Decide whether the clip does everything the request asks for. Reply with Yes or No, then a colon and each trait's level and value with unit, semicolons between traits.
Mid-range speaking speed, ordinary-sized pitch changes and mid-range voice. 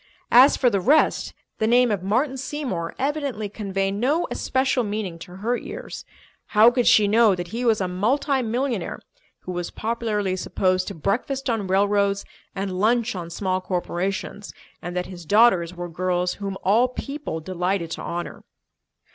No: average, 165 wpm; average, 4.7 semitones; high, 205 Hz